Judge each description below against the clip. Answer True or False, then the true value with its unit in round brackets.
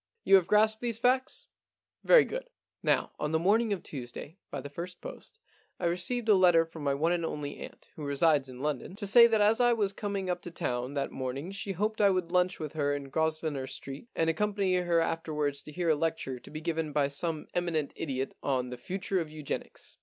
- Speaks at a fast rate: True (225 wpm)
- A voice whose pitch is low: False (165 Hz)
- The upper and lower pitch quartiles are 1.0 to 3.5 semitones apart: False (5.3 semitones)